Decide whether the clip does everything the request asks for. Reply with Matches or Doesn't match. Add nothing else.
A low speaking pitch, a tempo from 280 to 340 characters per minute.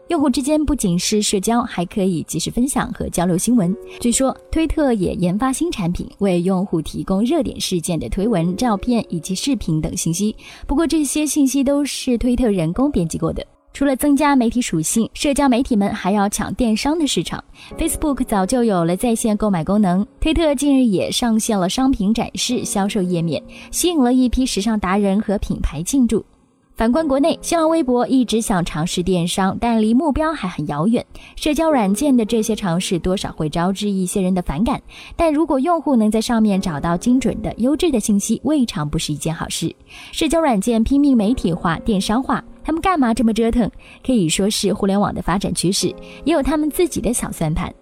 Doesn't match